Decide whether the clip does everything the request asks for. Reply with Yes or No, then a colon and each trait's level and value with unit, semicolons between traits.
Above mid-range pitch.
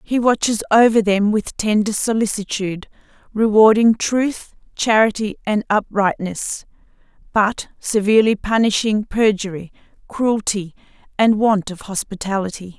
Yes: high, 210 Hz